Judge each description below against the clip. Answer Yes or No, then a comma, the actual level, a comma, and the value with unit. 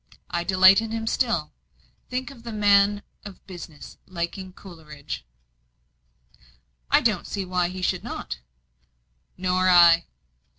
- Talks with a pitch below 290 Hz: Yes, medium, 185 Hz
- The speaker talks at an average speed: No, slow, 125 wpm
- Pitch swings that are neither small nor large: Yes, average, 3.1 semitones